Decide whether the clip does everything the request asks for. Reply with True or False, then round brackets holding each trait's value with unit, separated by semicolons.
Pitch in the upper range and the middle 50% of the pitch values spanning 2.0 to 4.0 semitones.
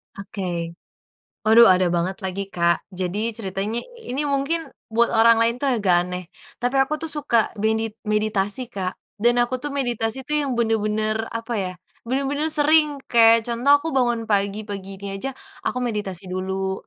False (225 Hz; 4.5 semitones)